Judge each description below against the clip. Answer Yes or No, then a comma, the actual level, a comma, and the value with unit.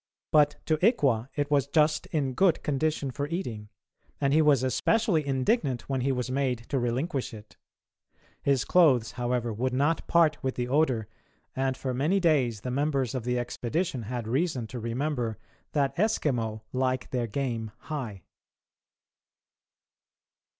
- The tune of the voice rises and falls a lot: No, average, 3.7 semitones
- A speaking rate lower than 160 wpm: Yes, average, 150 wpm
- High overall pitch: No, low, 135 Hz